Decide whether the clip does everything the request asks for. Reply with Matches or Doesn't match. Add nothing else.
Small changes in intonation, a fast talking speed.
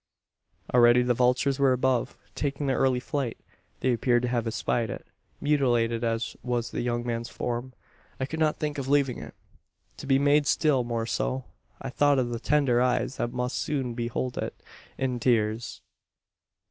Doesn't match